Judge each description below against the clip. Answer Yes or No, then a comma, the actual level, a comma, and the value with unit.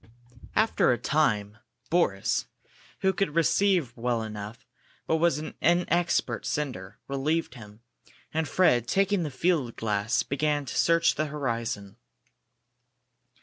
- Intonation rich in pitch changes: Yes, wide, 6.5 semitones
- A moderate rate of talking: No, slow, 120 wpm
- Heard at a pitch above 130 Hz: Yes, medium, 140 Hz